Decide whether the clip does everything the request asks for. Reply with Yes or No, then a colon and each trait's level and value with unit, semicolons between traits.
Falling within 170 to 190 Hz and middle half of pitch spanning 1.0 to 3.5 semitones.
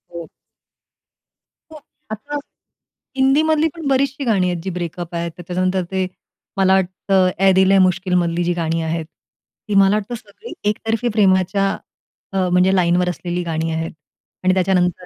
Yes: medium, 185 Hz; average, 2.9 semitones